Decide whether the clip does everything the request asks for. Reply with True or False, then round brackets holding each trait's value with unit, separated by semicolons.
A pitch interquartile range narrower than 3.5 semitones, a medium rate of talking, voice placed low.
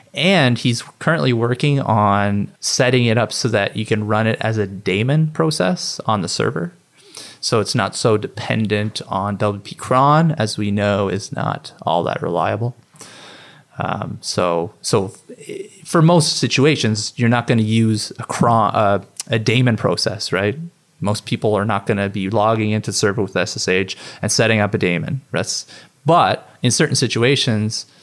False (4.3 semitones; 165 wpm; 110 Hz)